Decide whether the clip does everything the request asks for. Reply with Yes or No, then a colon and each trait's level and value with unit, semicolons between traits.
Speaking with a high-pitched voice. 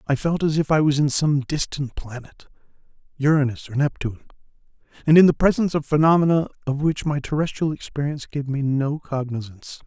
No: medium, 145 Hz